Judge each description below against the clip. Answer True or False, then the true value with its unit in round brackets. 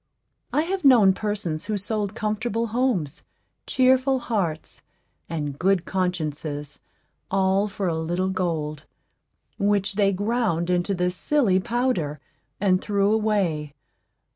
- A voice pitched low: False (195 Hz)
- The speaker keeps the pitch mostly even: False (4.1 semitones)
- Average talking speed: False (115 wpm)